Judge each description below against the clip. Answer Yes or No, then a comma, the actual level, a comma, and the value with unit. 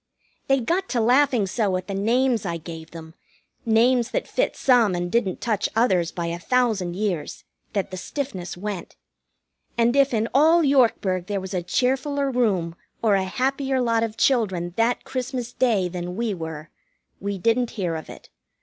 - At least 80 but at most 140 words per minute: No, average, 175 wpm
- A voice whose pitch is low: No, high, 220 Hz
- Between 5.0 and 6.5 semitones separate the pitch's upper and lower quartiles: Yes, wide, 5.6 semitones